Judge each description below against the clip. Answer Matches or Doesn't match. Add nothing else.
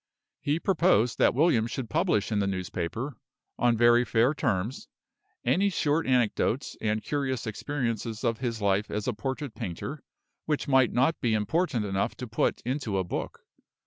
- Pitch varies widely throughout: Doesn't match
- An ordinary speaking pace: Matches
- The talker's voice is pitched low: Matches